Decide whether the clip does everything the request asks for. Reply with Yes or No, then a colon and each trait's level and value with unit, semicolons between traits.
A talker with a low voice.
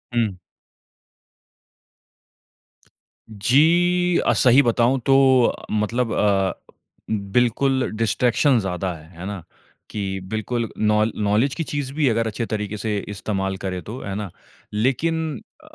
Yes: low, 110 Hz